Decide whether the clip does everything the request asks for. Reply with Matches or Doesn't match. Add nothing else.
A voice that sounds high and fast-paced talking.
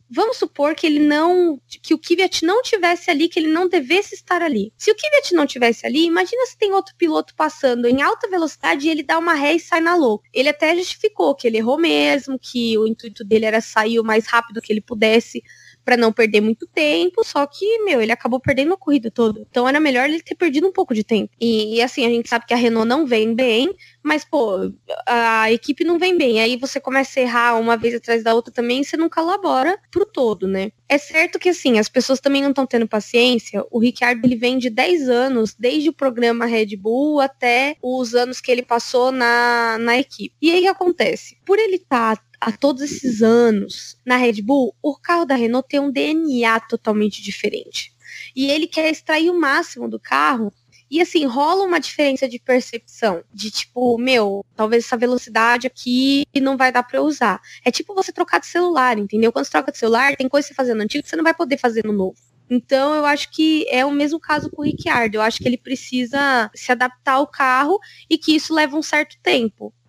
Matches